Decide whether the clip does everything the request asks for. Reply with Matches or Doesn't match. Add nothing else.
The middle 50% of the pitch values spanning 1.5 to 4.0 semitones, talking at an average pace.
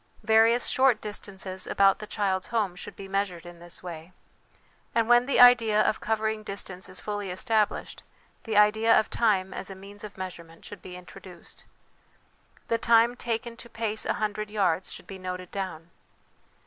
Matches